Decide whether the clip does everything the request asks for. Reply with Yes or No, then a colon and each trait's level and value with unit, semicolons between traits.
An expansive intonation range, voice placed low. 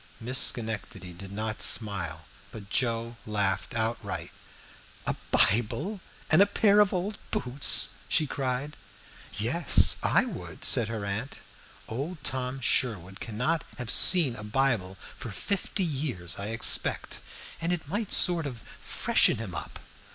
Yes: wide, 6.3 semitones; low, 120 Hz